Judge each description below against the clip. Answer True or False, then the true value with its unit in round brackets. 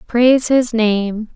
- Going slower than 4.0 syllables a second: True (3.5 syllables/s)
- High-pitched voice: True (230 Hz)